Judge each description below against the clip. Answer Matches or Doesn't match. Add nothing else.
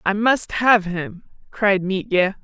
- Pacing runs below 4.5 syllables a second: Matches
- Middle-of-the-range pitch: Doesn't match